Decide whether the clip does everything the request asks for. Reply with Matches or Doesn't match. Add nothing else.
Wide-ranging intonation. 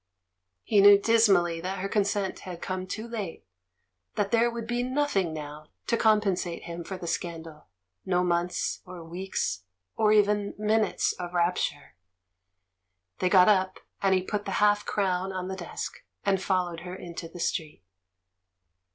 Doesn't match